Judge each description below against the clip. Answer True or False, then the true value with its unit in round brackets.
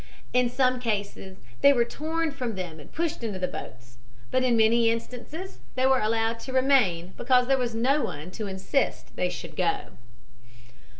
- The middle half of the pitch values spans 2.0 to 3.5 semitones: False (4.6 semitones)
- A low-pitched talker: False (240 Hz)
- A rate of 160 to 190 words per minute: True (175 wpm)